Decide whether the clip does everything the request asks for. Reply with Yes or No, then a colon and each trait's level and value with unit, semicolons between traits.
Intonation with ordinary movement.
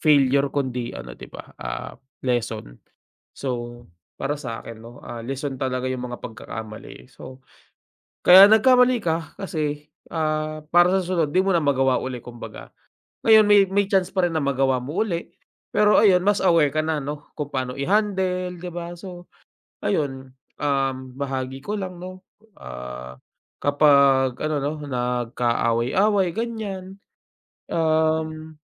No: wide, 5.8 semitones